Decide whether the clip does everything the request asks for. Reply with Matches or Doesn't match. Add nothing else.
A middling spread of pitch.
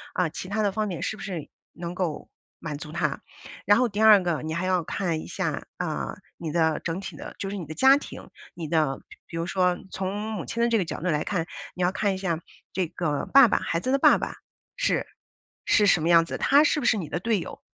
Matches